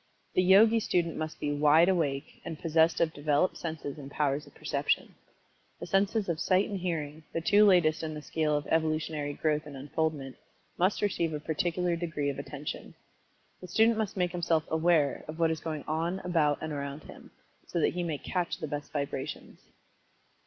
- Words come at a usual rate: Yes, average, 185 wpm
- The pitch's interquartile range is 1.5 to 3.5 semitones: Yes, average, 2.9 semitones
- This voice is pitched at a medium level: Yes, medium, 160 Hz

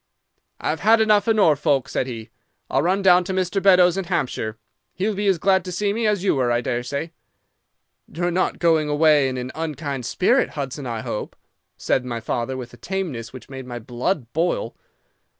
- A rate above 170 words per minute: Yes, average, 190 wpm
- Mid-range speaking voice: Yes, medium, 155 Hz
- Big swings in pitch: Yes, wide, 6.9 semitones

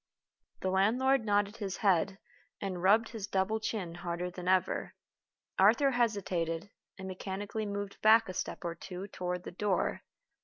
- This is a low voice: No, high, 195 Hz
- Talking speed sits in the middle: Yes, average, 155 wpm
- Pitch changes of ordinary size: Yes, average, 3.0 semitones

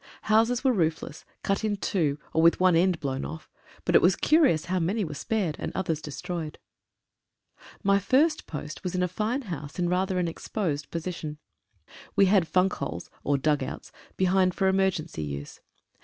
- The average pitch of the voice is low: No, medium, 180 Hz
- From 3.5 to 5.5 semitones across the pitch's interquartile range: Yes, average, 4.0 semitones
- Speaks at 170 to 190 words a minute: Yes, average, 180 wpm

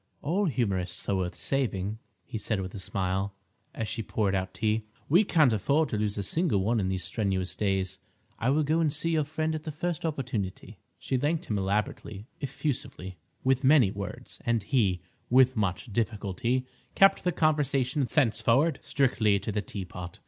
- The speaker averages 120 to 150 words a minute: No, average, 175 wpm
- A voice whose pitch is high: No, low, 115 Hz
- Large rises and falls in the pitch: Yes, wide, 6.7 semitones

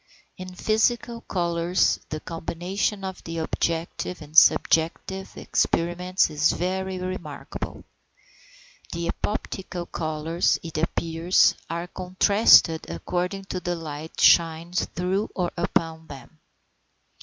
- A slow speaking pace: Yes, slow, 105 wpm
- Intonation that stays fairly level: Yes, narrow, 2.2 semitones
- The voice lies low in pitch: No, medium, 175 Hz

